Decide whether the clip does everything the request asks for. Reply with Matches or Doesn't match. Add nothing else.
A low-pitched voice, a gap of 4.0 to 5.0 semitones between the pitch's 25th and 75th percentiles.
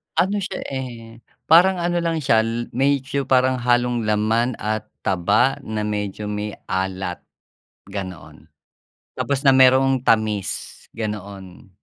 Matches